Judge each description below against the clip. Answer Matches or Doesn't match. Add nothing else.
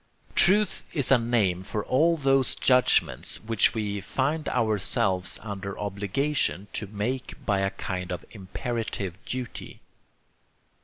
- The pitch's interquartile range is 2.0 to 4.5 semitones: Doesn't match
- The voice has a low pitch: Matches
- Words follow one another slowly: Matches